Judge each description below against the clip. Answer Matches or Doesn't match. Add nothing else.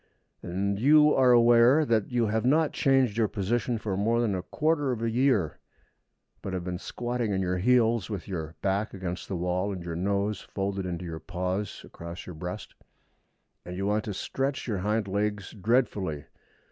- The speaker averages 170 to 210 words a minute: Matches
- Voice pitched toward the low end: Matches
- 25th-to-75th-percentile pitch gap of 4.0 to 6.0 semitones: Matches